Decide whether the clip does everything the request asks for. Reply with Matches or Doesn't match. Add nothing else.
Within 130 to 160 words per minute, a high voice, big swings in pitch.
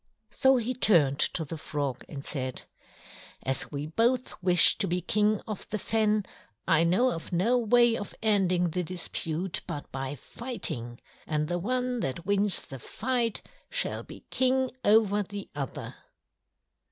Matches